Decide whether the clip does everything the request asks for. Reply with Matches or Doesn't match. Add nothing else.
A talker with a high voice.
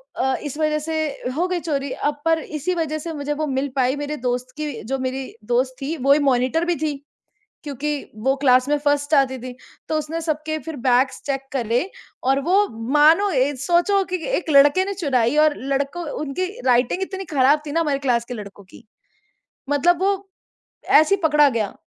Matches